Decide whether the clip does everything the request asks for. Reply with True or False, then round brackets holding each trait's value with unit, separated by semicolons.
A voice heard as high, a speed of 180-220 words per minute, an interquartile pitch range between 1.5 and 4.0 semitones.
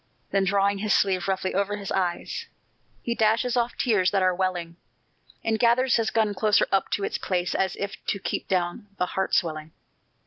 True (195 Hz; 185 wpm; 2.8 semitones)